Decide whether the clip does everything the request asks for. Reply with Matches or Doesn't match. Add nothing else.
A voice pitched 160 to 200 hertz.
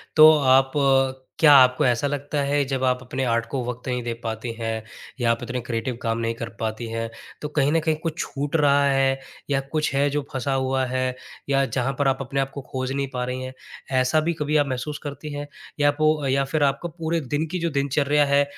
Doesn't match